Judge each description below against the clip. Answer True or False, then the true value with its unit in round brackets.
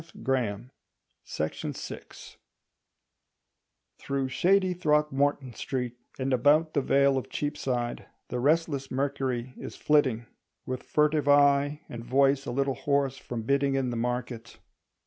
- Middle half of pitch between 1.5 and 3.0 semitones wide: True (2.5 semitones)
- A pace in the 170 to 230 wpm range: False (135 wpm)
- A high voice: False (135 Hz)